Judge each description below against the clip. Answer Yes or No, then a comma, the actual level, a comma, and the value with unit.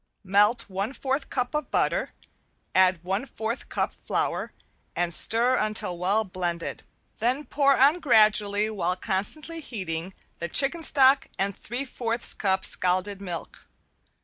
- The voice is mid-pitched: No, high, 210 Hz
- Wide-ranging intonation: Yes, wide, 5.8 semitones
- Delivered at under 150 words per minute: Yes, slow, 135 wpm